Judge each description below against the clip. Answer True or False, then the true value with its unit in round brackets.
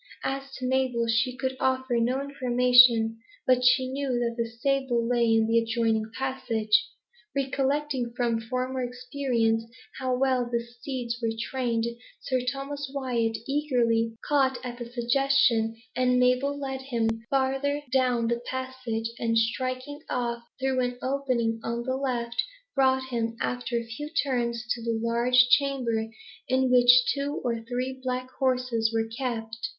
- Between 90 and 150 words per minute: True (145 wpm)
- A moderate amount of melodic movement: False (2.1 semitones)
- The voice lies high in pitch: True (250 Hz)